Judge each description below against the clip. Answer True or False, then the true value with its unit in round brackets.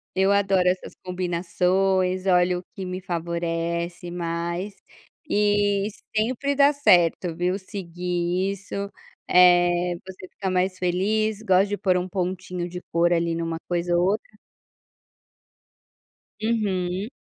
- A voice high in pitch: False (180 Hz)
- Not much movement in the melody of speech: True (2.0 semitones)